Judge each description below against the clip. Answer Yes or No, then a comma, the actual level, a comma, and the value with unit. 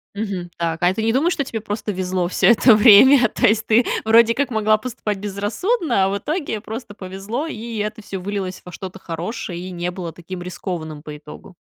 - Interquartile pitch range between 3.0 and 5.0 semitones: Yes, average, 3.9 semitones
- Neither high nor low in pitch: No, high, 205 Hz